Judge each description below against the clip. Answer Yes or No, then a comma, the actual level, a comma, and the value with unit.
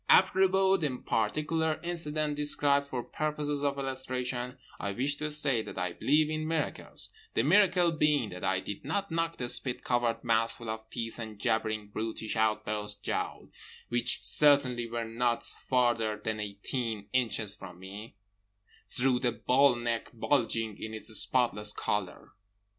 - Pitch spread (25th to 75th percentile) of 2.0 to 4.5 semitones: No, average, 5.0 semitones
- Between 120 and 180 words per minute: Yes, average, 145 wpm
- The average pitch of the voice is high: No, low, 120 Hz